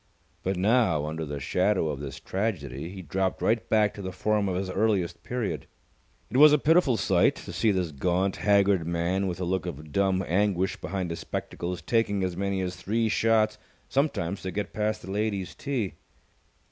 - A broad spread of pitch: No, average, 3.4 semitones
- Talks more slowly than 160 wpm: No, average, 185 wpm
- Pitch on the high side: No, very low, 95 Hz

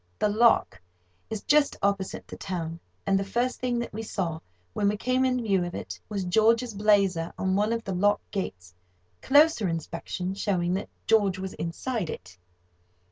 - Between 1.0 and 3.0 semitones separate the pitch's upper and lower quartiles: No, average, 4.0 semitones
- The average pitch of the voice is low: No, high, 200 Hz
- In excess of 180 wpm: No, average, 175 wpm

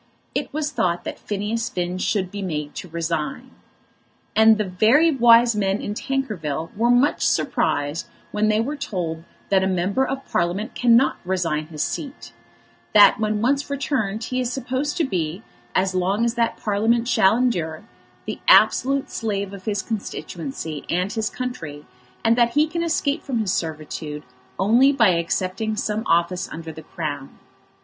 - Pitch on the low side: No, high, 210 Hz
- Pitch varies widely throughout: Yes, wide, 5.7 semitones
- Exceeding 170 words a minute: No, average, 160 wpm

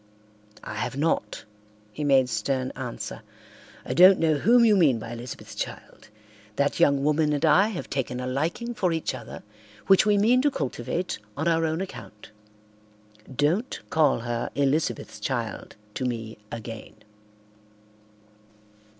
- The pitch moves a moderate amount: No, wide, 5.8 semitones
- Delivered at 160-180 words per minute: No, average, 140 wpm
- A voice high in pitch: No, medium, 145 Hz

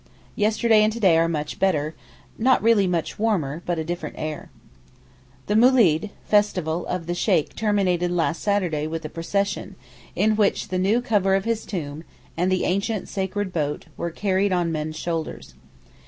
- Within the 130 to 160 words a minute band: No, average, 170 wpm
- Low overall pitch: No, medium, 185 Hz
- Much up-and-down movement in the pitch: No, average, 4.1 semitones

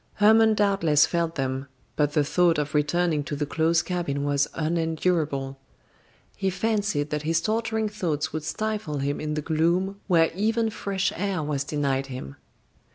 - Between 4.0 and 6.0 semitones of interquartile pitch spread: Yes, average, 4.9 semitones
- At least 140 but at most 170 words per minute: Yes, average, 160 wpm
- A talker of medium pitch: Yes, medium, 165 Hz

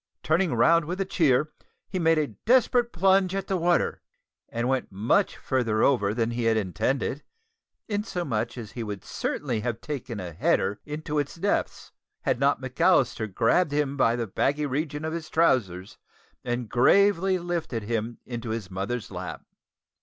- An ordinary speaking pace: Yes, average, 160 wpm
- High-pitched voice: No, low, 135 Hz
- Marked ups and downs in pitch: Yes, wide, 6.7 semitones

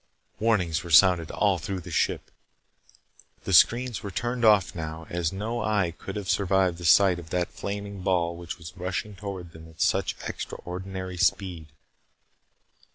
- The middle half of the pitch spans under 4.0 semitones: Yes, average, 2.9 semitones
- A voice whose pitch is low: Yes, very low, 95 Hz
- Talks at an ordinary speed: Yes, average, 160 wpm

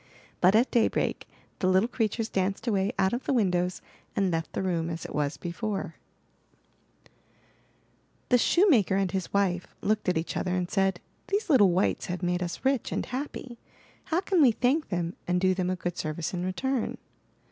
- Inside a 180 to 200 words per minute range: Yes, average, 190 wpm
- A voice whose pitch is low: No, high, 190 Hz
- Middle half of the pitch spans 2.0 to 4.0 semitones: No, average, 4.8 semitones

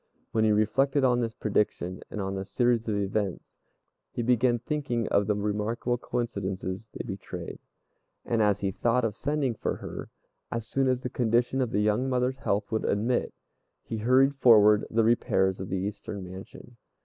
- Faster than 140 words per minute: Yes, average, 175 wpm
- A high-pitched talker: No, low, 110 Hz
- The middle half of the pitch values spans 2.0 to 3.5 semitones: Yes, average, 3.2 semitones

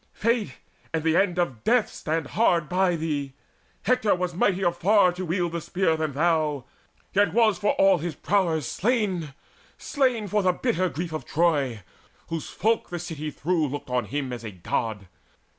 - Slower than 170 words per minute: No, average, 175 wpm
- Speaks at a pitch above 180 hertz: No, medium, 170 Hz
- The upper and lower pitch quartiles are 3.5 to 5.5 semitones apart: Yes, average, 4.3 semitones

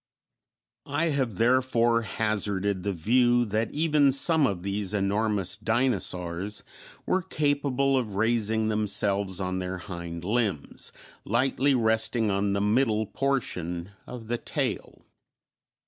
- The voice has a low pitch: Yes, low, 110 Hz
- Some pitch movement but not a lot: Yes, average, 4.2 semitones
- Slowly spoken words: Yes, slow, 115 wpm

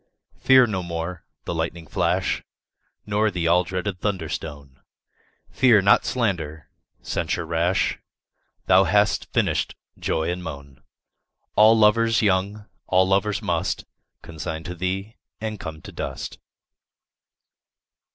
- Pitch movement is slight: No, average, 4.2 semitones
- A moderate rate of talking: No, slow, 120 wpm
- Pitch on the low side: Yes, very low, 90 Hz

